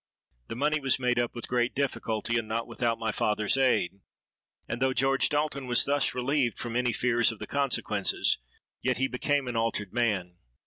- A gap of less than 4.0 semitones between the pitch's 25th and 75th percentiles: Yes, average, 2.8 semitones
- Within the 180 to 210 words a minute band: Yes, average, 185 wpm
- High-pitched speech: No, low, 120 Hz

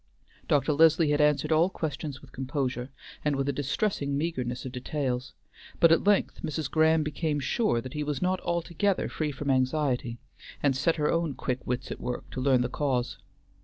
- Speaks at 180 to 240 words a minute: Yes, average, 185 wpm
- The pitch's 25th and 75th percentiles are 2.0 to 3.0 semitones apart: No, average, 3.5 semitones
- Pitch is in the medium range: Yes, medium, 145 Hz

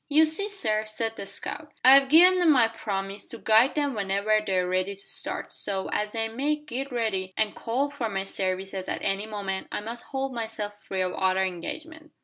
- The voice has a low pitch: No, high, 220 Hz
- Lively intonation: Yes, wide, 5.8 semitones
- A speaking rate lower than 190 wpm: No, average, 200 wpm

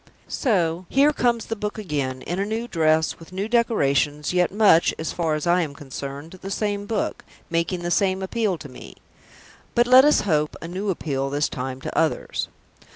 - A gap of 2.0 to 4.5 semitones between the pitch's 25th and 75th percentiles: No, wide, 5.6 semitones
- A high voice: No, medium, 175 Hz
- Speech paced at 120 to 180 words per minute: No, average, 190 wpm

